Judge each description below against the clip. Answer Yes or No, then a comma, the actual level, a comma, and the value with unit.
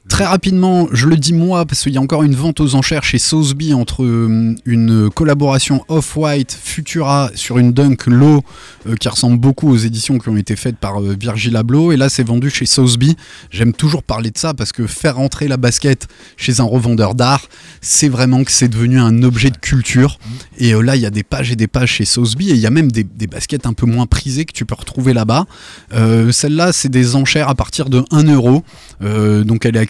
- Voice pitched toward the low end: Yes, low, 125 Hz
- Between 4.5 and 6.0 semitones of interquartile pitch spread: No, average, 3.8 semitones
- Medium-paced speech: No, fast, 230 wpm